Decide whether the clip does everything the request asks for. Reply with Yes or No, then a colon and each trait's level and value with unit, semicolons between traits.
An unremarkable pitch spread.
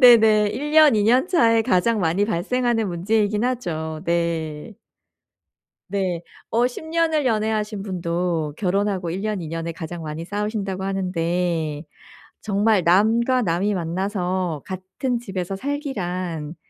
Yes: average, 4.5 semitones